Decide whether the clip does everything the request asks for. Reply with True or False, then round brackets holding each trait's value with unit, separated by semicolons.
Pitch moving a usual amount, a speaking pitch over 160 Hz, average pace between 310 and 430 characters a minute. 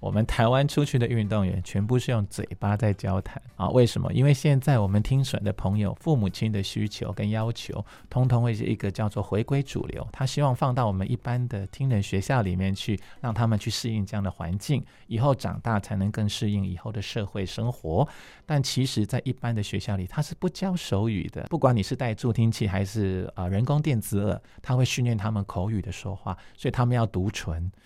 False (4.0 semitones; 110 Hz; 325 characters per minute)